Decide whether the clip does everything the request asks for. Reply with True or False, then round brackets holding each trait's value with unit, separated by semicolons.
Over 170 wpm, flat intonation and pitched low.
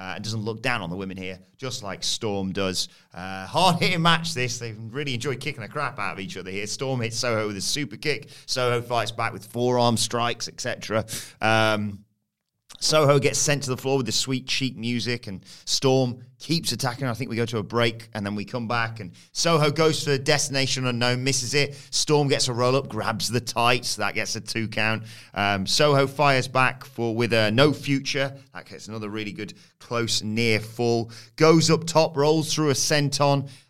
False (205 wpm; 4.1 semitones; 120 Hz)